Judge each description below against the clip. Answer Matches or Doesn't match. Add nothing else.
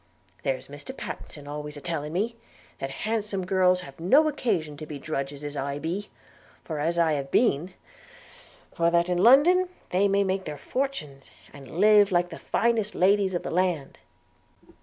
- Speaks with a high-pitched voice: Doesn't match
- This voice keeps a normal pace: Matches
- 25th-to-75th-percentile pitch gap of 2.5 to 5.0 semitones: Doesn't match